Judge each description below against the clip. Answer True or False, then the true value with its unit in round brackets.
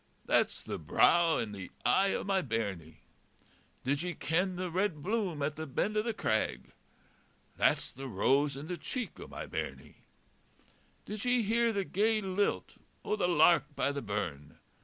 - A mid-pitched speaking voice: True (175 Hz)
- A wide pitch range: True (6.9 semitones)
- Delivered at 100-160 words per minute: False (170 wpm)